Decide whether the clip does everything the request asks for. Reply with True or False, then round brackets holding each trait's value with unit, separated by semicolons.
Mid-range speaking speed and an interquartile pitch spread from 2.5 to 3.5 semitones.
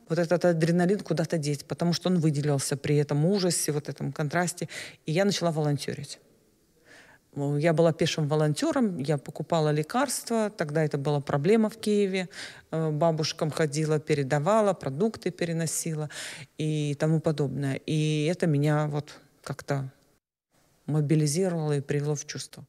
True (130 wpm; 2.8 semitones)